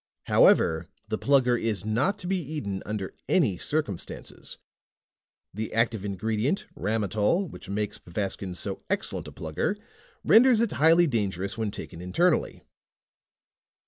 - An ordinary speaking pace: No, slow, 125 wpm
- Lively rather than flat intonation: Yes, wide, 7.9 semitones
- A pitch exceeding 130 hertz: No, low, 110 Hz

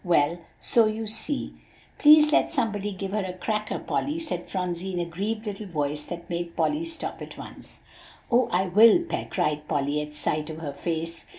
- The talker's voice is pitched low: No, medium, 185 Hz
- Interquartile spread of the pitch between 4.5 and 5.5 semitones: Yes, average, 4.9 semitones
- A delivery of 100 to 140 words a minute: No, average, 190 wpm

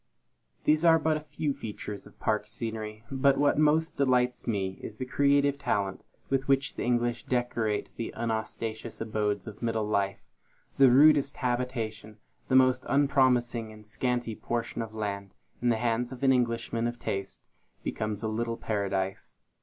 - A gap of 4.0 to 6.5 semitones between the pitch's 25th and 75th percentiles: No, average, 3.4 semitones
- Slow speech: No, average, 165 wpm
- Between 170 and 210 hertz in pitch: No, low, 120 Hz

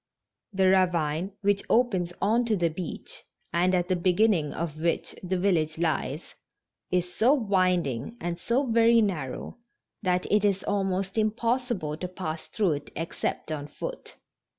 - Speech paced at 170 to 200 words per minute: No, average, 145 wpm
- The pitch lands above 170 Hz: Yes, medium, 185 Hz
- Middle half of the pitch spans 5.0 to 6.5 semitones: No, average, 3.7 semitones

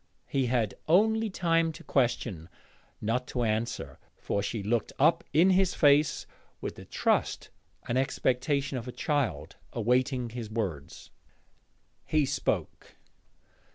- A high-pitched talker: No, low, 125 Hz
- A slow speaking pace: Yes, slow, 125 wpm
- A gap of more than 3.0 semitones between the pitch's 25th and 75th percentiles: Yes, average, 5.1 semitones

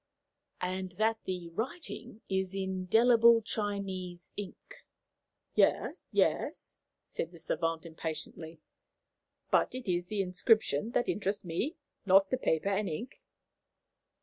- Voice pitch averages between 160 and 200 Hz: Yes, high, 190 Hz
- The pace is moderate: No, slow, 120 wpm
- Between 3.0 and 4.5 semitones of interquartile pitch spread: Yes, average, 3.7 semitones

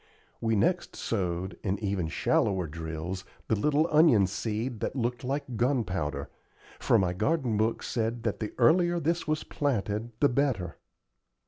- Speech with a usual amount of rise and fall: No, wide, 6.5 semitones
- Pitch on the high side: No, low, 115 Hz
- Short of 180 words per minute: Yes, average, 145 wpm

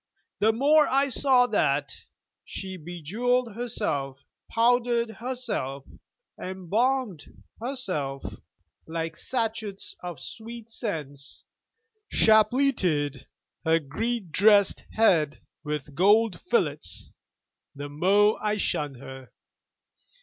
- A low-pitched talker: No, high, 205 Hz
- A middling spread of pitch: No, wide, 7.7 semitones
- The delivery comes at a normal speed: No, slow, 90 wpm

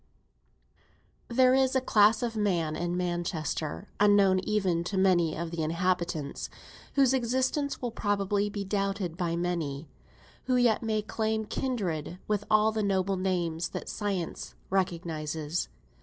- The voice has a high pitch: Yes, high, 195 Hz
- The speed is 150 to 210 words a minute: No, average, 140 wpm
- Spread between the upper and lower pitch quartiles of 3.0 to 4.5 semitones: Yes, average, 4.0 semitones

